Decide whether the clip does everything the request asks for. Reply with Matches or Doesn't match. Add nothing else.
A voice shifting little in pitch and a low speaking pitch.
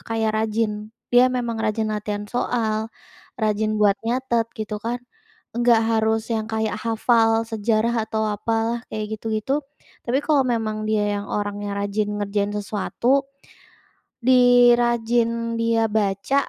Doesn't match